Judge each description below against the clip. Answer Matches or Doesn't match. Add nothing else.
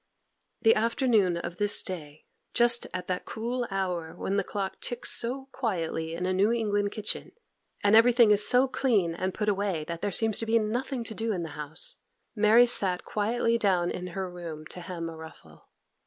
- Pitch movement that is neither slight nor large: Matches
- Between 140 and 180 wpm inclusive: Doesn't match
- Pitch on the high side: Matches